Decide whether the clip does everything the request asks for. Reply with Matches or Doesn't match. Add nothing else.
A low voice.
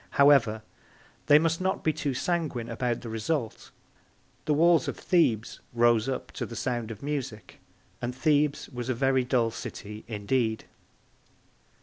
Matches